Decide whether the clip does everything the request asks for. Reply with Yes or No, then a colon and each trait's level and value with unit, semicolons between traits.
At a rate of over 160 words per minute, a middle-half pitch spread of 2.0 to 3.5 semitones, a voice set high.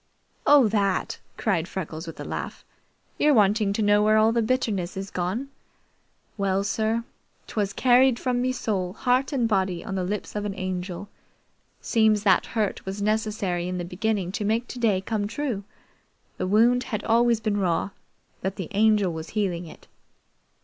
Yes: average, 170 wpm; average, 3.1 semitones; high, 210 Hz